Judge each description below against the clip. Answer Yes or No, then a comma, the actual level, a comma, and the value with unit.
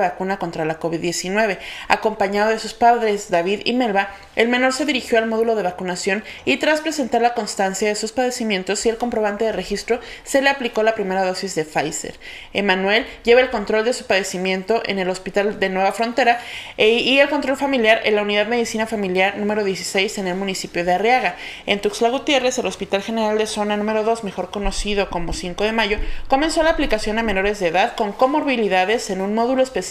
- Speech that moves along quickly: Yes, fast, 200 wpm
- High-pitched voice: Yes, high, 215 Hz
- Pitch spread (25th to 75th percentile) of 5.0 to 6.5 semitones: No, average, 3.4 semitones